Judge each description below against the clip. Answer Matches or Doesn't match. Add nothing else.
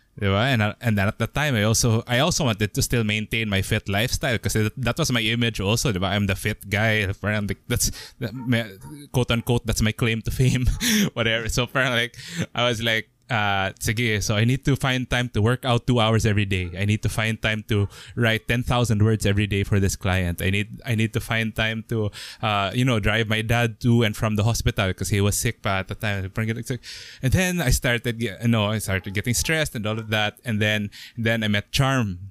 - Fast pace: Matches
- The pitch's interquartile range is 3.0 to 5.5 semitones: Doesn't match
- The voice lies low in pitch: Matches